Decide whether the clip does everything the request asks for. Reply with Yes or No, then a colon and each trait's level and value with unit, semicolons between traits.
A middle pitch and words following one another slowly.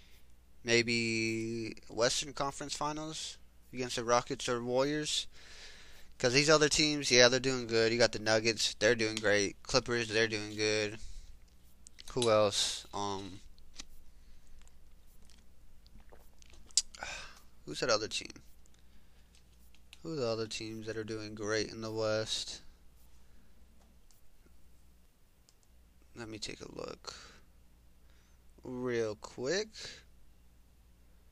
No: very low, 85 Hz; slow, 100 wpm